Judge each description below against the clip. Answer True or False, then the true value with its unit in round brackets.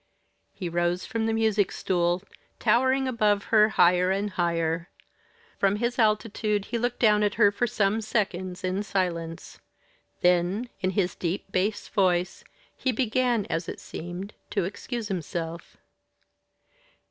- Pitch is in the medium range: False (200 Hz)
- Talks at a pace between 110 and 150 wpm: True (135 wpm)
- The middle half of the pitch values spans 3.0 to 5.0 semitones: True (3.6 semitones)